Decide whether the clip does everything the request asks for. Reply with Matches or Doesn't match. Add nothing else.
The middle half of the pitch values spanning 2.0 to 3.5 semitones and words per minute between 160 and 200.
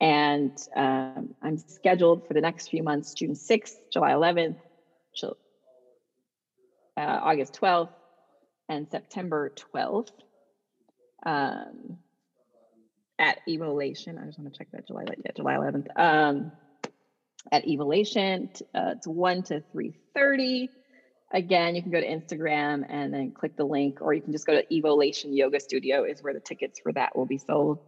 Doesn't match